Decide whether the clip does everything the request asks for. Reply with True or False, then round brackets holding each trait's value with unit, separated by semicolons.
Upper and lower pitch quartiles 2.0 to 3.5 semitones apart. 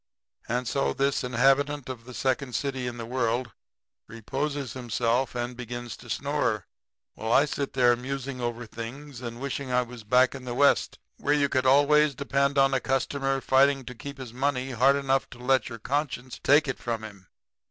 True (2.4 semitones)